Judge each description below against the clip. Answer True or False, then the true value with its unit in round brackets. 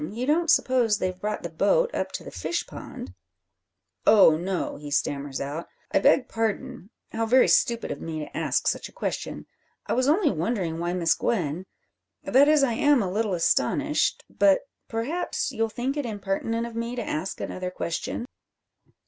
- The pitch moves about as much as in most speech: False (6.2 semitones)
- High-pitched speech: True (220 Hz)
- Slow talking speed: False (175 wpm)